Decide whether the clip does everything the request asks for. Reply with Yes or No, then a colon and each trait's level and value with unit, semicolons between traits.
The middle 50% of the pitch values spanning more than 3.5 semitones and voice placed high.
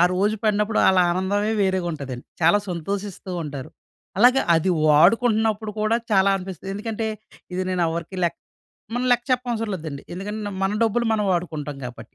Yes: average, 4.0 semitones; high, 195 Hz